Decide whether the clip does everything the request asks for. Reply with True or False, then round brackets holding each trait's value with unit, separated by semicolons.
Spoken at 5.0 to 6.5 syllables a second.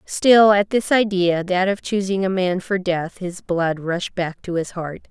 False (4.0 syllables/s)